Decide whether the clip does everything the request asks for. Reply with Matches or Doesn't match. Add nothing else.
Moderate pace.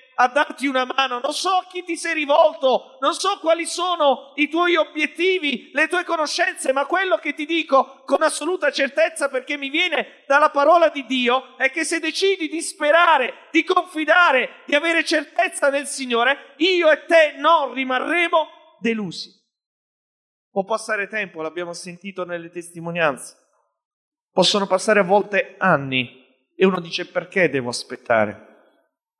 Matches